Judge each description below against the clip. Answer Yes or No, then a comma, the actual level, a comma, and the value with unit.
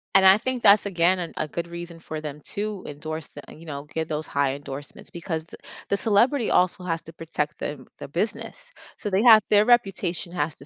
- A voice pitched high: No, medium, 170 Hz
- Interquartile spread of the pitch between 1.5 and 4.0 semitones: No, average, 4.7 semitones